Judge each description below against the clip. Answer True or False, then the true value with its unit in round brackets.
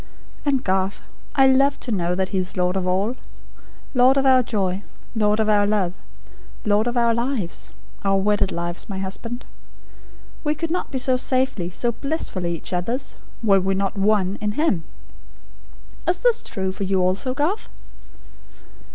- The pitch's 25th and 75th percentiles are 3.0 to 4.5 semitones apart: False (5.4 semitones)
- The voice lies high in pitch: True (210 Hz)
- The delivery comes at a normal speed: True (165 wpm)